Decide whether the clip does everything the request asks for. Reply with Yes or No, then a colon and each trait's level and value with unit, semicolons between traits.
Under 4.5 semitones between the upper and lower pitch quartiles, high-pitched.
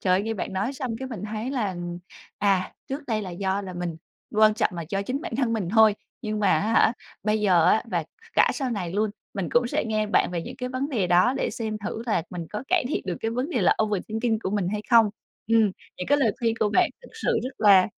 Yes: average, 4.1 semitones; high, 215 Hz